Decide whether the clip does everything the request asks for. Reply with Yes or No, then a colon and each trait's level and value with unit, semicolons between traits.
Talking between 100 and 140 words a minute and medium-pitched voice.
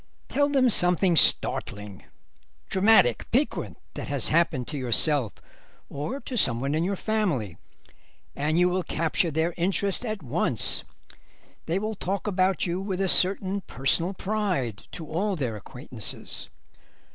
Yes: slow, 135 wpm; medium, 180 Hz